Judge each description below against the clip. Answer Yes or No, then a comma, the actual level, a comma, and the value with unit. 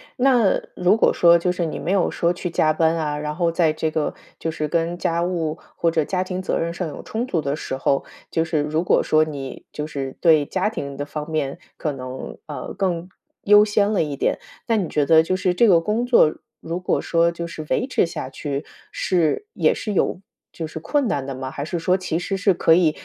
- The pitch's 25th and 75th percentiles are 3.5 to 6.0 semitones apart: No, average, 3.1 semitones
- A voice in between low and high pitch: Yes, medium, 165 Hz